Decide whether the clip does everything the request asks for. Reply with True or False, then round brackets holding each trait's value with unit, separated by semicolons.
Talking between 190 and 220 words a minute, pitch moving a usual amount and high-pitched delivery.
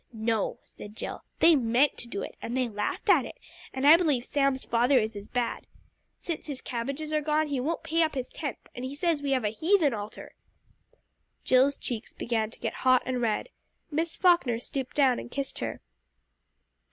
True (195 wpm; 4.1 semitones; 260 Hz)